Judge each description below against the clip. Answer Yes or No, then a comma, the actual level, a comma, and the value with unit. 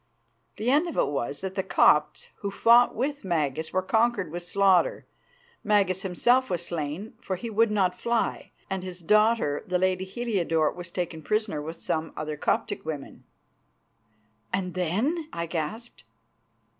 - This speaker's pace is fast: No, average, 155 wpm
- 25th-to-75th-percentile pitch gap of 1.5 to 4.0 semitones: No, average, 4.8 semitones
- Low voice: No, medium, 185 Hz